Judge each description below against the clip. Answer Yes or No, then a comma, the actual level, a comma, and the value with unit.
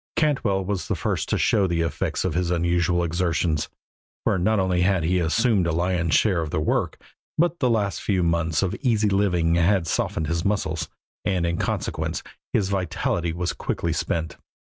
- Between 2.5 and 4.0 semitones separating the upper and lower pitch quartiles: Yes, average, 2.9 semitones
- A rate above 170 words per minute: Yes, average, 180 wpm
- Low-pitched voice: Yes, very low, 90 Hz